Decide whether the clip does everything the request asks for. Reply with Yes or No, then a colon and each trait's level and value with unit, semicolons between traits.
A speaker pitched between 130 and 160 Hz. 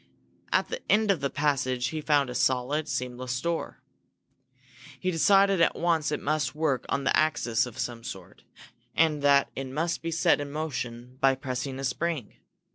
Yes: medium, 140 Hz